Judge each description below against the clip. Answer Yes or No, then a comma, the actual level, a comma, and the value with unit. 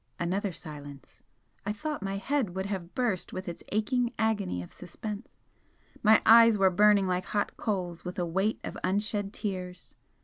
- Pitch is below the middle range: No, high, 195 Hz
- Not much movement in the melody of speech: No, average, 3.0 semitones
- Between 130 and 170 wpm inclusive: Yes, average, 165 wpm